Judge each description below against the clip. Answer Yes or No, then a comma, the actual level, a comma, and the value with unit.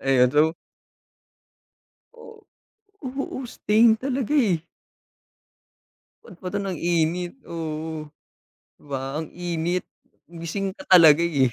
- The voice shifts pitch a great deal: No, average, 4.2 semitones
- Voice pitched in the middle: Yes, medium, 170 Hz